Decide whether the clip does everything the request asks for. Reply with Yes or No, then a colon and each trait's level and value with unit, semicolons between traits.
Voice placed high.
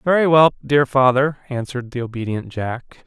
No: low, 130 Hz